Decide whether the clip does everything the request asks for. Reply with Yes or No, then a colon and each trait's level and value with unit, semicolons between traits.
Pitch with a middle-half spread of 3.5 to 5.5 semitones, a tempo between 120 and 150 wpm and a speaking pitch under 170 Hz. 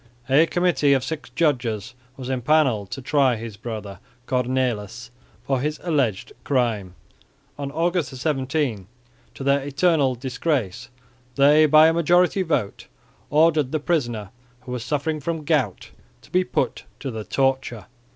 Yes: average, 4.3 semitones; average, 140 wpm; low, 135 Hz